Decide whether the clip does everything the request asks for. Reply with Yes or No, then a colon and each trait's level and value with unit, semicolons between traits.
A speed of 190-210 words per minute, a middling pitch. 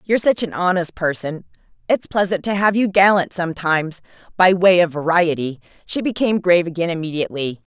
No: average, 165 wpm; medium, 180 Hz